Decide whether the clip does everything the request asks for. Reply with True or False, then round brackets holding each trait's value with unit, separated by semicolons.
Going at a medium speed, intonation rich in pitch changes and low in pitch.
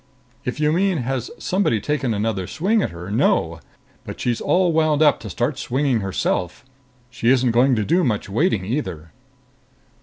True (170 wpm; 6.2 semitones; 125 Hz)